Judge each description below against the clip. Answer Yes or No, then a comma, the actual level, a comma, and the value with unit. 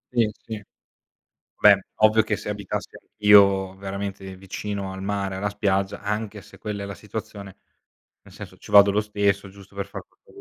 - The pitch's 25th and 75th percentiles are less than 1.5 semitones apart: Yes, narrow, 1.1 semitones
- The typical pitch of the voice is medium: No, low, 100 Hz